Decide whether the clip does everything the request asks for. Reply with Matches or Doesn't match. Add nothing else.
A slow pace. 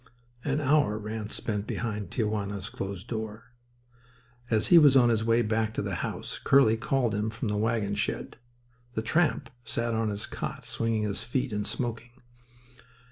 Doesn't match